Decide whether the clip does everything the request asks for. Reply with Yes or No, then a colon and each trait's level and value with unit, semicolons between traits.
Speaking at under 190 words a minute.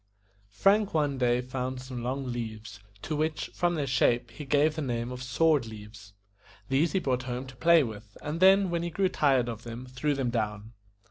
No: average, 200 wpm